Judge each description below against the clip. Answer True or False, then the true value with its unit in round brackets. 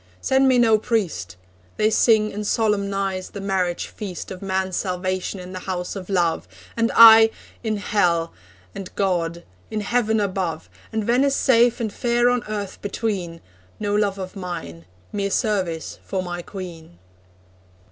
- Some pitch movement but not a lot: True (3.3 semitones)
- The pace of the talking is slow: False (150 wpm)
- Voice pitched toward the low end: False (200 Hz)